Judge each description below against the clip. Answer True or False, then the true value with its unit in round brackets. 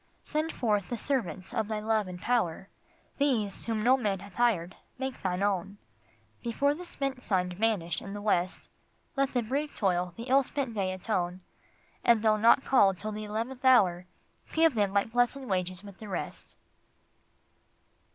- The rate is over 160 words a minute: True (170 wpm)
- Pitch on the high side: True (215 Hz)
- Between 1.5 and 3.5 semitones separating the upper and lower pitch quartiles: False (4.8 semitones)